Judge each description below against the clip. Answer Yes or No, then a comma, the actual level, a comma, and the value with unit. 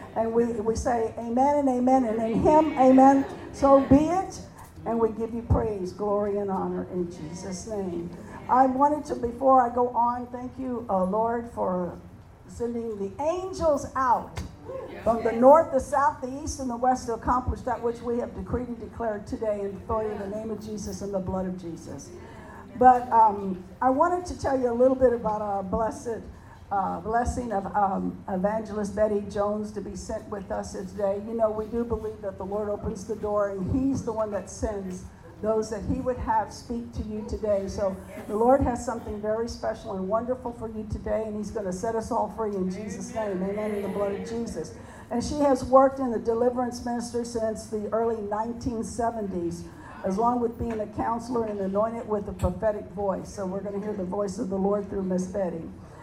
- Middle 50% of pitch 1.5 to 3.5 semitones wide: Yes, average, 3.0 semitones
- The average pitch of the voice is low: No, high, 220 Hz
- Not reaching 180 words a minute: No, fast, 205 wpm